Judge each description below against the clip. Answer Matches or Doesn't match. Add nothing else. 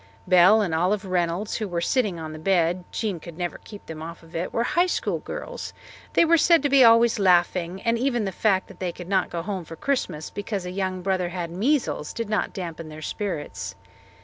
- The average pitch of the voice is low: Doesn't match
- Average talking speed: Doesn't match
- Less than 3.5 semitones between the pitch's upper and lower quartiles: Doesn't match